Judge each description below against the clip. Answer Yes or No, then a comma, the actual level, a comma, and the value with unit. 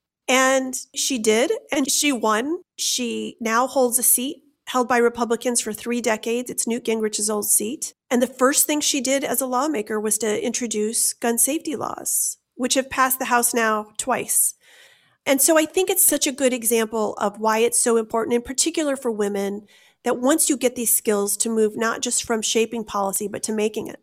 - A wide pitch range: No, average, 3.4 semitones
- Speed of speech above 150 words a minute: Yes, average, 195 wpm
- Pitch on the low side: No, high, 240 Hz